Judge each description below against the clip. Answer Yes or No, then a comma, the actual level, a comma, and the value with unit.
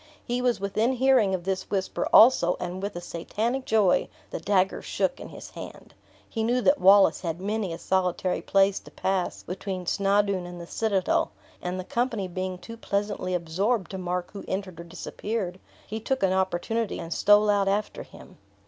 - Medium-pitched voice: No, high, 195 Hz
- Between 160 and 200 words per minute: Yes, average, 185 wpm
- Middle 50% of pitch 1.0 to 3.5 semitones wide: Yes, average, 2.9 semitones